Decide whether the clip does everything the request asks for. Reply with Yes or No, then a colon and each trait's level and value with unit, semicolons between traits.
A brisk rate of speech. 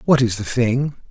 Yes: fast, 220 wpm